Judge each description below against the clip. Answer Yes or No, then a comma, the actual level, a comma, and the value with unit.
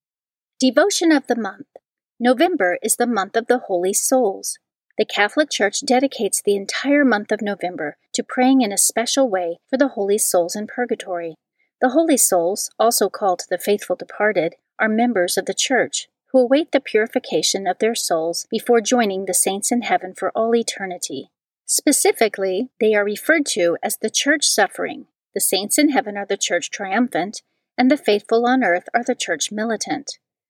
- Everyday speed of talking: Yes, average, 175 wpm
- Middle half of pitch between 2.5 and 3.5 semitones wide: No, average, 4.9 semitones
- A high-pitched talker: Yes, high, 220 Hz